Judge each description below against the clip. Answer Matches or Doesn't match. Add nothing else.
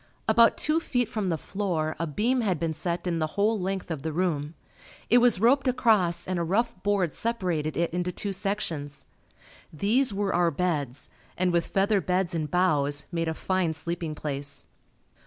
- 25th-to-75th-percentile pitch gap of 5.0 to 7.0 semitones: Doesn't match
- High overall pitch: Doesn't match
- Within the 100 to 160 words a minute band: Doesn't match